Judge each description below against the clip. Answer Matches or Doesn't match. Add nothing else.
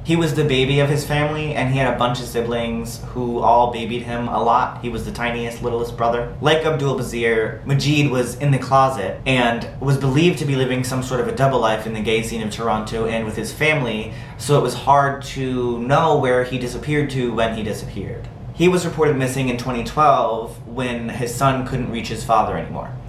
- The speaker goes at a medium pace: Doesn't match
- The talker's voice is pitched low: Matches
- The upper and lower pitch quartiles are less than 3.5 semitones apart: Matches